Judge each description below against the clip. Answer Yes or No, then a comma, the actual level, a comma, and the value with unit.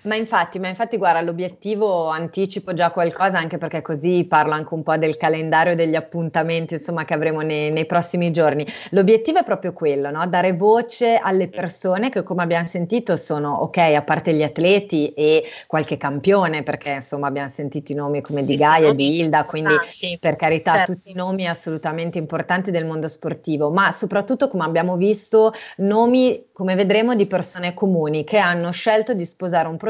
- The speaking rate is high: Yes, fast, 180 wpm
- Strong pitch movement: No, average, 3.2 semitones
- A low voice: No, medium, 170 Hz